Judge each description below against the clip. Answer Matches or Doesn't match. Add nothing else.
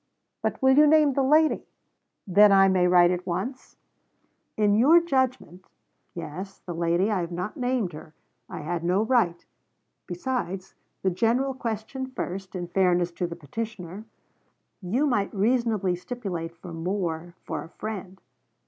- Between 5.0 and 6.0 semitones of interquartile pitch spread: Matches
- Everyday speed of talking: Matches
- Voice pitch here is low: Doesn't match